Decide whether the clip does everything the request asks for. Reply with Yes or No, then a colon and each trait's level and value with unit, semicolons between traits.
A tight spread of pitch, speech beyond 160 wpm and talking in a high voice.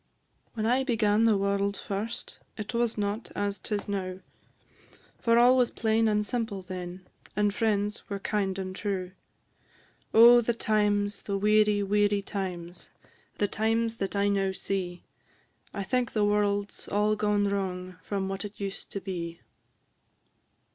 No: narrow, 1.8 semitones; average, 150 wpm; high, 205 Hz